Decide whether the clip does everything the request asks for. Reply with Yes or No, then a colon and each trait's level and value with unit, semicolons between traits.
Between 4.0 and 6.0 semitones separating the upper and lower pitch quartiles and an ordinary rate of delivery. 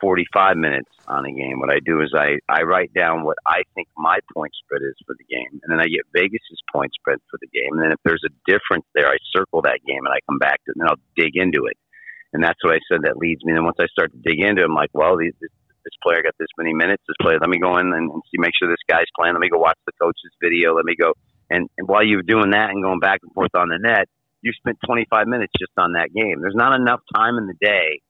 No: average, 4.9 semitones; fast, 290 wpm